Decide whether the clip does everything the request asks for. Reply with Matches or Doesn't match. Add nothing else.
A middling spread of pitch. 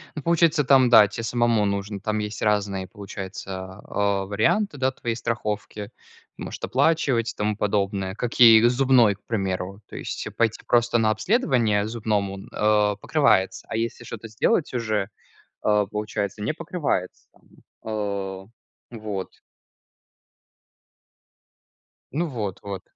Matches